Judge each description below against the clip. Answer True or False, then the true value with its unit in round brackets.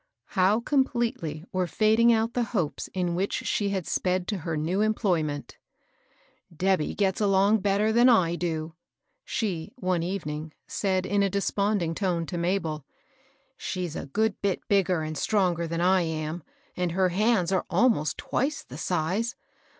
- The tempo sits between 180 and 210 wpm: False (160 wpm)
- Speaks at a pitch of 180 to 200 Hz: True (185 Hz)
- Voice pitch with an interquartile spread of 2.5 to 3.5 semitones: False (3.9 semitones)